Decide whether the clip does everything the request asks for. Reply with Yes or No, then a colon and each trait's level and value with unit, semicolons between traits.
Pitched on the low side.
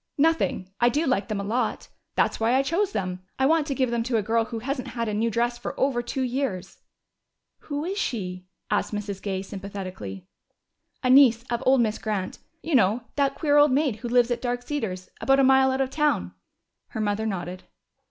No: high, 240 Hz